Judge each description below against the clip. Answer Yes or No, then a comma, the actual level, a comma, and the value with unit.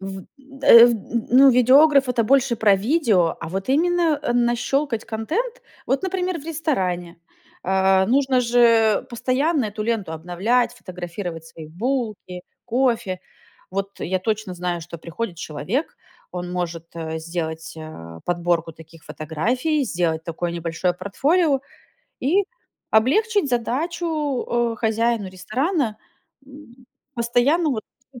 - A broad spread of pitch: Yes, wide, 7.1 semitones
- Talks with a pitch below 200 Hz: No, high, 225 Hz